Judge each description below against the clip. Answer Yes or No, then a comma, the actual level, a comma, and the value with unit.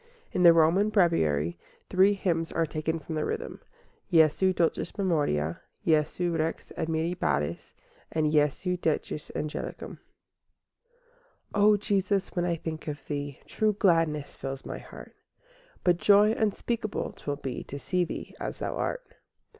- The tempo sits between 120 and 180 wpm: Yes, average, 140 wpm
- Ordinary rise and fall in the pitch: Yes, average, 4.0 semitones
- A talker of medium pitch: Yes, medium, 165 Hz